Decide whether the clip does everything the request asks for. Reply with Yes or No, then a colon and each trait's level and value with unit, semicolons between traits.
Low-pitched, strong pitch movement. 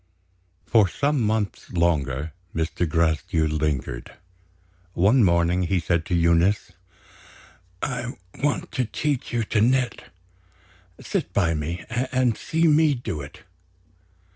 Yes: very low, 90 Hz; wide, 6.7 semitones